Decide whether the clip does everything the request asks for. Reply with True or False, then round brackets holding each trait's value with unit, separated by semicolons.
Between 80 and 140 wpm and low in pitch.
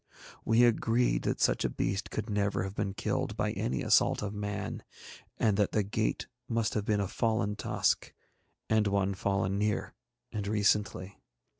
False (165 wpm; 105 Hz)